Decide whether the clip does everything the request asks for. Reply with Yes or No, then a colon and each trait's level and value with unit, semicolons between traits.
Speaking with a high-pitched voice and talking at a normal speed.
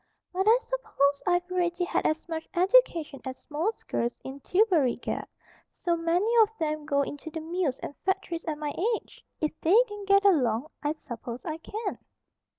Yes: very high, 330 Hz; average, 175 wpm